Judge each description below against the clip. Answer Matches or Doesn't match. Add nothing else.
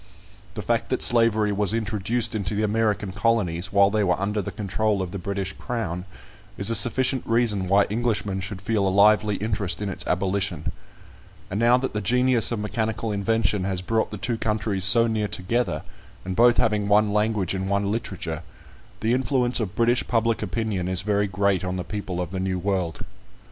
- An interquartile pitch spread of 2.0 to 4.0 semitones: Matches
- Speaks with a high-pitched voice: Doesn't match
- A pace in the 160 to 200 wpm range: Matches